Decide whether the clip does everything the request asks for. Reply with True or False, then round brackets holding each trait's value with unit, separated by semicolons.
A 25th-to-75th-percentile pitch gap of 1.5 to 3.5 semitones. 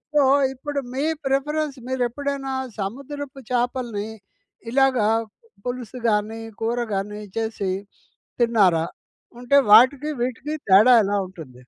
False (4.4 semitones)